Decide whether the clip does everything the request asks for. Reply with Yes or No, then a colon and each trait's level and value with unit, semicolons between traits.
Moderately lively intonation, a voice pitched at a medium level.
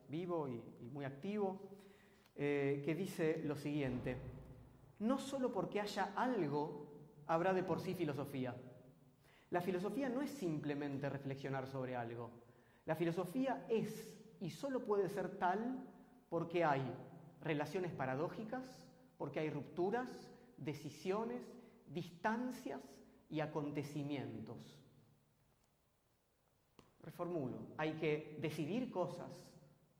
No: wide, 5.8 semitones; medium, 165 Hz